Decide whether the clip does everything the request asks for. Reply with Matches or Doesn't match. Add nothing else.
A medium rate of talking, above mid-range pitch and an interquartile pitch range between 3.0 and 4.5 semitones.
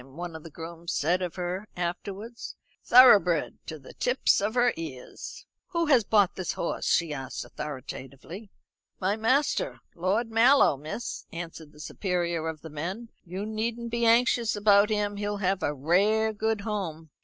Doesn't match